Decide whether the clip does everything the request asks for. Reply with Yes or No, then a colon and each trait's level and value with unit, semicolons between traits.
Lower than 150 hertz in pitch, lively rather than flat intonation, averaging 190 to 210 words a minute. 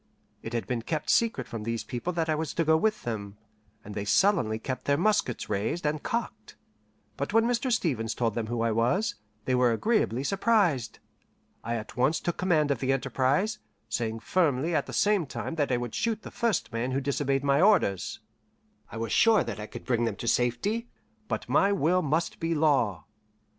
Yes: medium, 140 Hz; wide, 7.5 semitones; average, 200 wpm